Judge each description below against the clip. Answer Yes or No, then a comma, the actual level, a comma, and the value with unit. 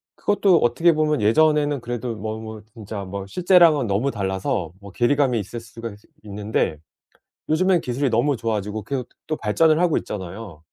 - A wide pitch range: Yes, wide, 6.3 semitones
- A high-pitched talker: No, low, 115 Hz